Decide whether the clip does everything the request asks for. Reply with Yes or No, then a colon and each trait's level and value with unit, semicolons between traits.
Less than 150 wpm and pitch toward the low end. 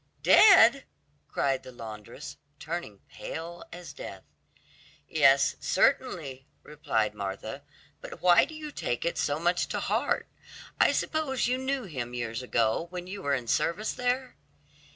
No: average, 140 wpm; medium, 170 Hz